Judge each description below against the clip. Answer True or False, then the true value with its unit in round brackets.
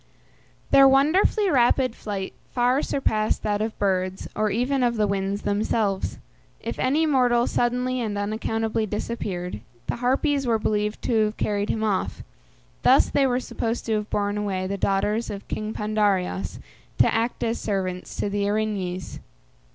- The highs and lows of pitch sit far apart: False (3.2 semitones)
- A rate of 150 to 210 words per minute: True (155 wpm)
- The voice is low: False (215 Hz)